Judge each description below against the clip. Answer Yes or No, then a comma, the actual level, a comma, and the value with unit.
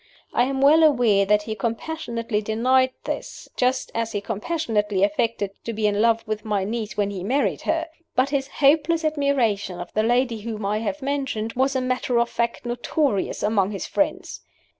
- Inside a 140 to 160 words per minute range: No, average, 185 wpm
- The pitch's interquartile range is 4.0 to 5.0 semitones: Yes, average, 4.3 semitones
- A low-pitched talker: No, high, 230 Hz